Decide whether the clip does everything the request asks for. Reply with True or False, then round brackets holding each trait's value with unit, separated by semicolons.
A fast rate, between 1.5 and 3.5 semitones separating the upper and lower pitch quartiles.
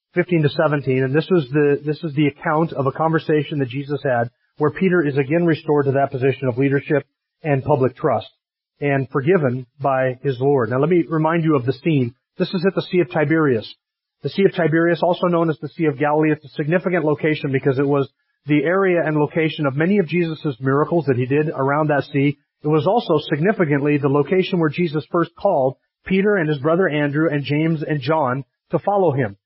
True (215 wpm; 3.1 semitones)